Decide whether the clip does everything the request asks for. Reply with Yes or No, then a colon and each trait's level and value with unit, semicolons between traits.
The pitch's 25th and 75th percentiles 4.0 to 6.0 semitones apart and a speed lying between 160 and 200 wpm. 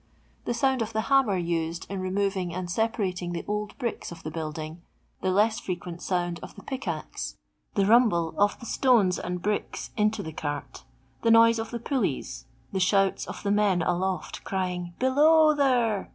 Yes: average, 4.6 semitones; average, 190 wpm